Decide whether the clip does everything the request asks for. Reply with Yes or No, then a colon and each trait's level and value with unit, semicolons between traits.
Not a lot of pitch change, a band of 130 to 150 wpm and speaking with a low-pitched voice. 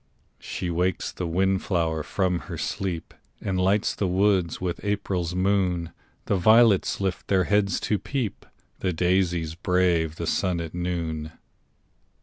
Yes: narrow, 2.3 semitones; average, 140 wpm; very low, 90 Hz